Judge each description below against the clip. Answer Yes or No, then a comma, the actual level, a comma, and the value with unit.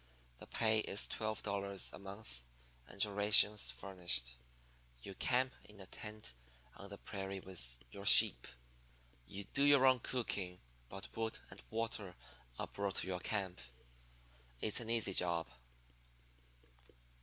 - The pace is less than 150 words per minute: Yes, average, 140 wpm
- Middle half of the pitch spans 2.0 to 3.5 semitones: Yes, average, 2.7 semitones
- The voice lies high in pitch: No, low, 100 Hz